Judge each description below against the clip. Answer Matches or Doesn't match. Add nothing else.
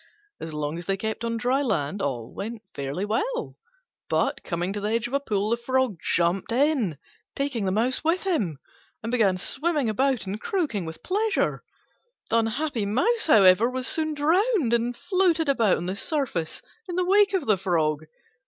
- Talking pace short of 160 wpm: Doesn't match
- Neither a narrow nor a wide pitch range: Doesn't match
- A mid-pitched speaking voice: Doesn't match